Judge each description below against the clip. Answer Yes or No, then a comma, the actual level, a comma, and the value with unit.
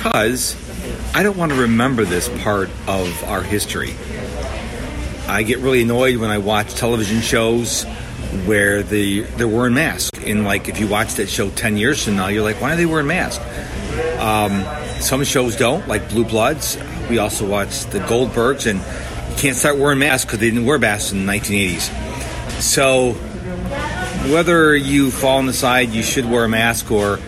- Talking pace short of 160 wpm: No, average, 180 wpm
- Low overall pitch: Yes, low, 115 Hz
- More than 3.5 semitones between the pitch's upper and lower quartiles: Yes, average, 4.1 semitones